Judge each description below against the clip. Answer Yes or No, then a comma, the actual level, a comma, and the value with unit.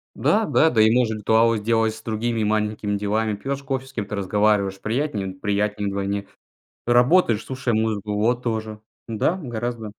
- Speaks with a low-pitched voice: Yes, low, 110 Hz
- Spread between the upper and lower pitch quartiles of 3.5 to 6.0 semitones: No, narrow, 2.5 semitones